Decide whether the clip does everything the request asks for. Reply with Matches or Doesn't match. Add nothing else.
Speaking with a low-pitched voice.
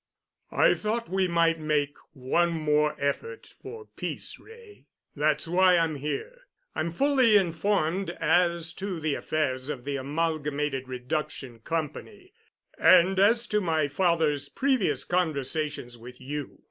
Doesn't match